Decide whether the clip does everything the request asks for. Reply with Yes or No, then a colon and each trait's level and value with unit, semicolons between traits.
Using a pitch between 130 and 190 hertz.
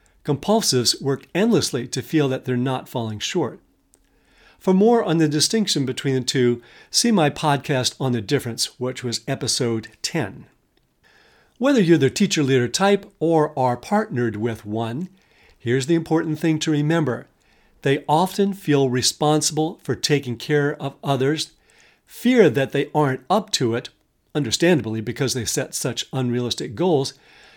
Yes: medium, 140 Hz